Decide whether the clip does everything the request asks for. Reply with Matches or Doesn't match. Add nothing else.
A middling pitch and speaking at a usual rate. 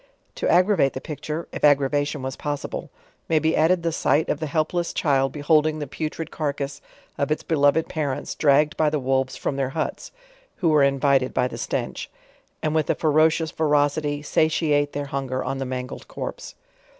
Matches